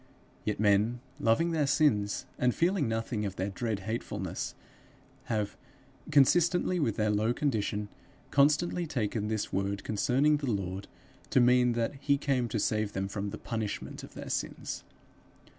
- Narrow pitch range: No, wide, 5.4 semitones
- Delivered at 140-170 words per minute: Yes, average, 150 wpm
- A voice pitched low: Yes, low, 115 Hz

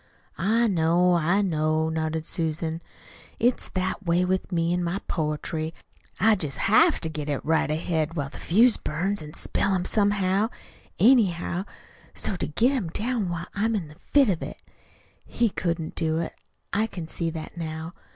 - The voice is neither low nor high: Yes, medium, 175 Hz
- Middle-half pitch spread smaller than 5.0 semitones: Yes, average, 4.0 semitones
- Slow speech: No, average, 170 wpm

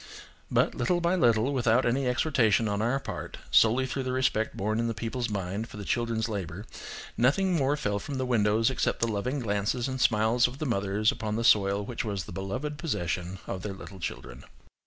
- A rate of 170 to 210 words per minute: Yes, average, 200 wpm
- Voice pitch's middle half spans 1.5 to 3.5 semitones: No, average, 4.0 semitones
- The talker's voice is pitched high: No, low, 115 Hz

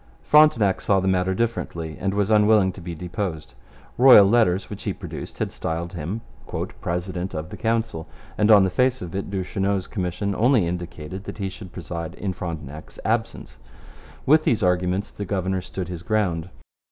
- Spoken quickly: No, average, 170 wpm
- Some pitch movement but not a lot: Yes, average, 3.0 semitones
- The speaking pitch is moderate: No, very low, 95 Hz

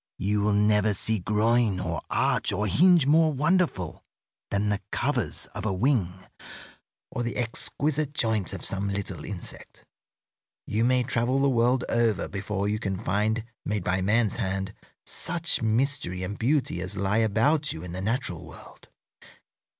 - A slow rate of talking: No, average, 155 wpm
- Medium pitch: No, low, 105 Hz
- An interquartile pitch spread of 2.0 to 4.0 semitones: No, average, 4.4 semitones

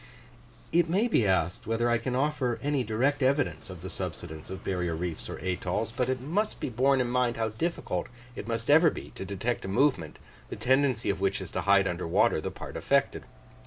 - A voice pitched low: Yes, low, 115 Hz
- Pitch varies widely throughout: Yes, wide, 6.1 semitones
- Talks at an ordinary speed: No, fast, 210 wpm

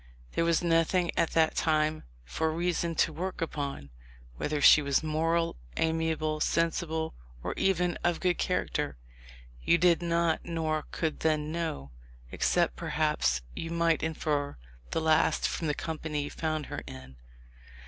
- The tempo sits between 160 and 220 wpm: No, average, 145 wpm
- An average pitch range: No, narrow, 1.6 semitones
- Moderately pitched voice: Yes, medium, 160 Hz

